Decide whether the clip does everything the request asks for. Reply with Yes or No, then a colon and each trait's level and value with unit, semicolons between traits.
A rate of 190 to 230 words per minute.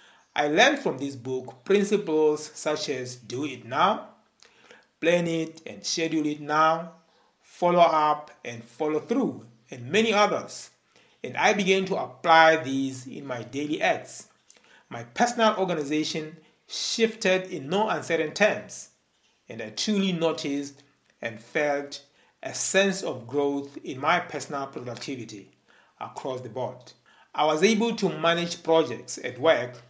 No: slow, 135 wpm